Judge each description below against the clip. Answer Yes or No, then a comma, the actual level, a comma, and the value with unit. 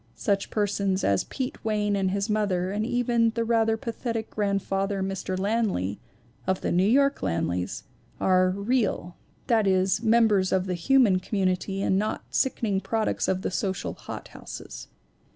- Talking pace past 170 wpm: No, average, 150 wpm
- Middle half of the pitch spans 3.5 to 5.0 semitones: No, average, 3.0 semitones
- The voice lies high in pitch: Yes, high, 200 Hz